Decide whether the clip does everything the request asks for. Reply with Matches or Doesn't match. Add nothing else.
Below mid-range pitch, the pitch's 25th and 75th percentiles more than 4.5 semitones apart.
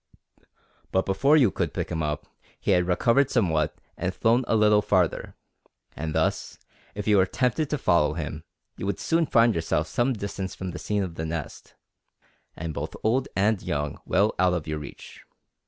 Matches